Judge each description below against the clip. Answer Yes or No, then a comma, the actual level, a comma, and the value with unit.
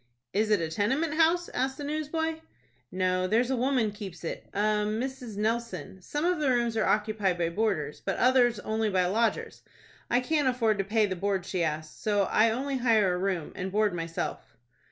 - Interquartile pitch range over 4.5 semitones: Yes, average, 5.0 semitones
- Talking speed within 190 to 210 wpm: Yes, average, 195 wpm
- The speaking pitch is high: Yes, high, 215 Hz